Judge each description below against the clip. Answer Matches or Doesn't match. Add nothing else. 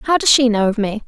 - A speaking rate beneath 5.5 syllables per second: Matches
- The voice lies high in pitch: Matches